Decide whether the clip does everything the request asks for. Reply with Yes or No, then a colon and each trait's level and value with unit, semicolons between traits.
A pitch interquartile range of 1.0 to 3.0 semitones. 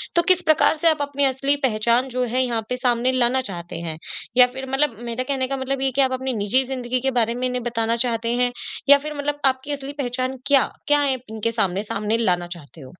Yes: average, 2.7 semitones